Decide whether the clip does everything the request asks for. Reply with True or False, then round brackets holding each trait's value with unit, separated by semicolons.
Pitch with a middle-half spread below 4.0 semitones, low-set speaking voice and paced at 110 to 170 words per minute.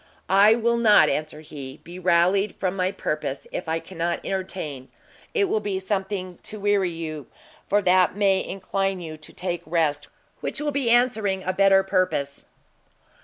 False (3.4 semitones; 185 Hz; 165 wpm)